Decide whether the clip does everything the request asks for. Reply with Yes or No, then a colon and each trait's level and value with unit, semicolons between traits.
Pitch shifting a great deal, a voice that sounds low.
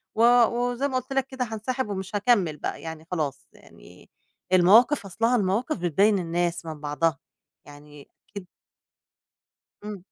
No: wide, 6.3 semitones; high, 195 Hz